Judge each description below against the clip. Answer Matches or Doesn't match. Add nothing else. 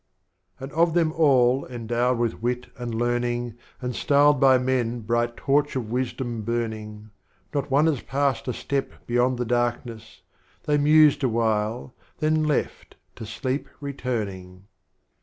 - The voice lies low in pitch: Matches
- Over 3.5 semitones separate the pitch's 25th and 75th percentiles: Doesn't match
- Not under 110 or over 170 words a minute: Matches